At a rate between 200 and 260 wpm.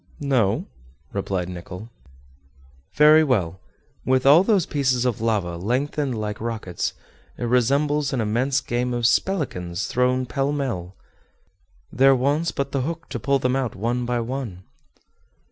No: slow, 135 wpm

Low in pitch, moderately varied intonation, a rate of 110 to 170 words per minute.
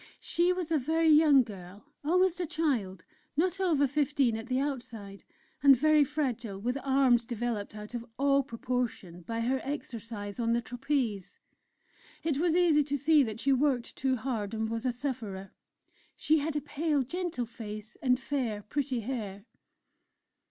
No: very high, 255 Hz; average, 4.6 semitones; average, 160 wpm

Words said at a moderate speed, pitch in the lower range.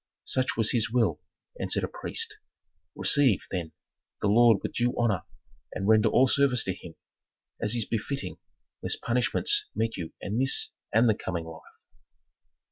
Yes: average, 155 wpm; low, 115 Hz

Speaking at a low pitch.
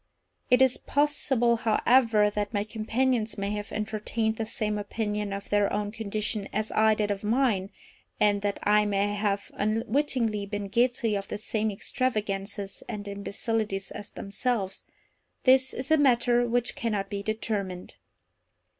No: high, 215 Hz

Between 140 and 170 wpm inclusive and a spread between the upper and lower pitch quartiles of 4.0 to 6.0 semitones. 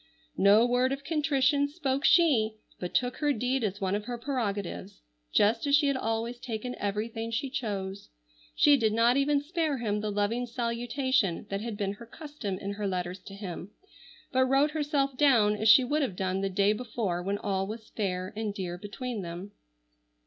No: average, 185 wpm; average, 4.8 semitones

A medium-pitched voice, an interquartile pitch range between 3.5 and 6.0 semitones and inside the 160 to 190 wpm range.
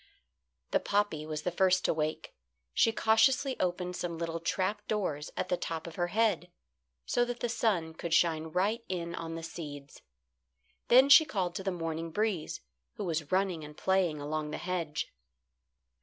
Yes: medium, 175 Hz; average, 4.1 semitones; average, 170 wpm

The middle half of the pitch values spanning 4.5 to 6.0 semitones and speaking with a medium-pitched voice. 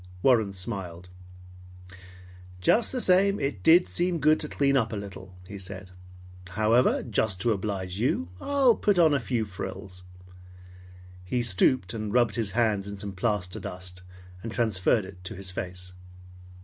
No: average, 5.1 semitones; low, 105 Hz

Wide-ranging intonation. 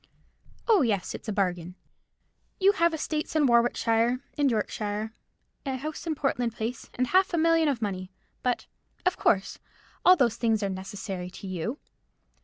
Yes: wide, 6.8 semitones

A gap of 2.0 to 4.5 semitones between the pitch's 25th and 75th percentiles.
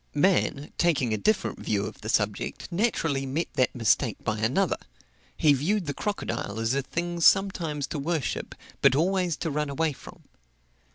No: average, 4.9 semitones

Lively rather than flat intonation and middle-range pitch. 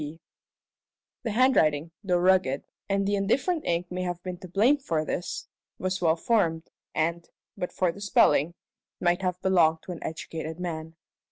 No: average, 2.8 semitones; medium, 175 Hz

